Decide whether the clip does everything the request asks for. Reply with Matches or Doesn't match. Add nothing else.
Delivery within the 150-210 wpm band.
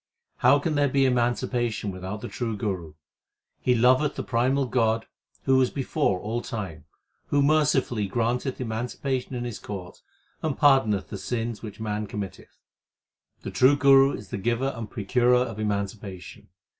Matches